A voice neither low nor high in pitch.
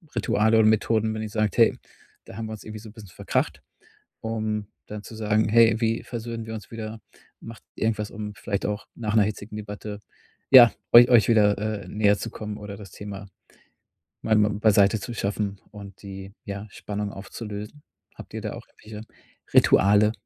No: low, 105 Hz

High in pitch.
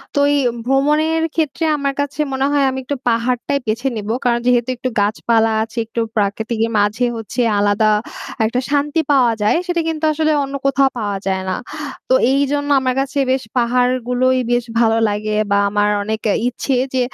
Yes: very high, 250 Hz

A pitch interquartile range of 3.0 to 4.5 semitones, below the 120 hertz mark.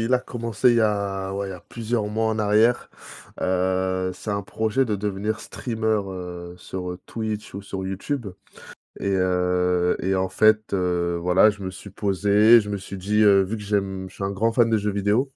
No: narrow, 2.6 semitones; low, 100 Hz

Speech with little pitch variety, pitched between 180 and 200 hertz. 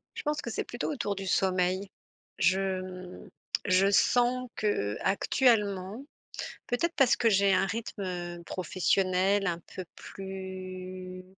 Yes: narrow, 2.3 semitones; high, 190 Hz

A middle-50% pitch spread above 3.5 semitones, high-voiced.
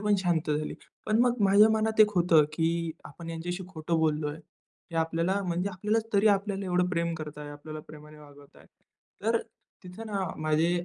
No: average, 4.2 semitones; medium, 170 Hz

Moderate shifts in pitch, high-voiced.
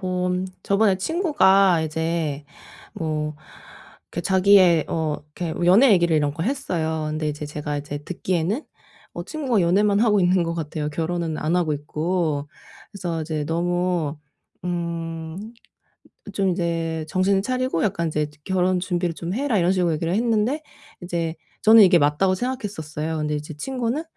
No: average, 3.5 semitones; medium, 175 Hz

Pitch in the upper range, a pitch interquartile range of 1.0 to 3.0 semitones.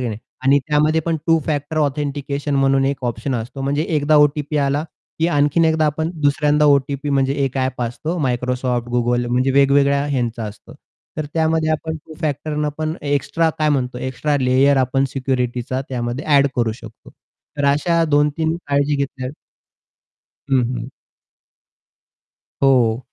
No: medium, 140 Hz; average, 2.7 semitones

